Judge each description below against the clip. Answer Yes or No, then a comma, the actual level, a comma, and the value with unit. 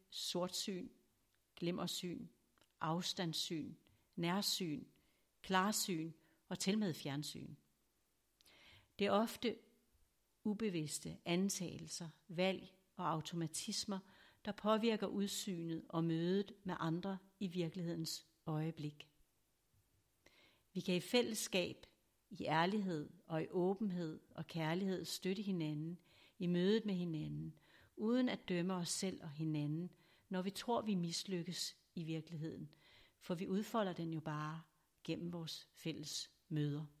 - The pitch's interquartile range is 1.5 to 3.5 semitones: Yes, average, 3.2 semitones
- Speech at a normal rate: No, slow, 110 wpm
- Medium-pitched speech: Yes, medium, 175 Hz